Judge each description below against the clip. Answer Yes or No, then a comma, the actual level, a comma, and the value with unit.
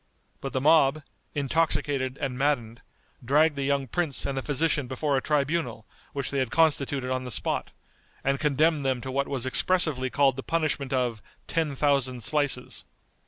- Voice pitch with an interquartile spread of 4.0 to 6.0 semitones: No, narrow, 2.4 semitones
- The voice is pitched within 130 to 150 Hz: Yes, medium, 140 Hz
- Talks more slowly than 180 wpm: Yes, average, 165 wpm